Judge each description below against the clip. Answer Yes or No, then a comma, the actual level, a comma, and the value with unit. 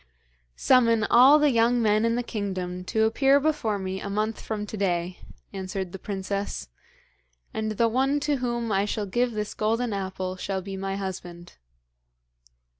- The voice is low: No, high, 210 Hz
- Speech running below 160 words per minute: No, average, 165 wpm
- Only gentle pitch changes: No, average, 3.6 semitones